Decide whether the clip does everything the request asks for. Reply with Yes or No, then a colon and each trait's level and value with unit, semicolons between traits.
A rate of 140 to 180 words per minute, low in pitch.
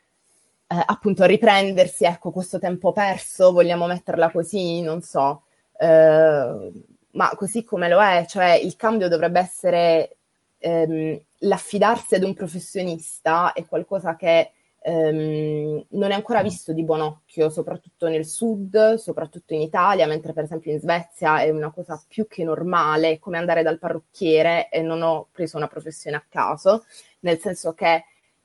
No: average, 150 wpm; medium, 170 Hz